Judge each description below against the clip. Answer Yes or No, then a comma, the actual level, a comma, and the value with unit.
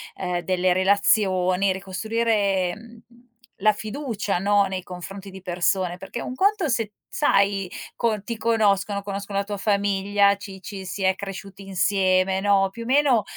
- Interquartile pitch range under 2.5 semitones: Yes, narrow, 2.0 semitones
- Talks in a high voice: Yes, high, 200 Hz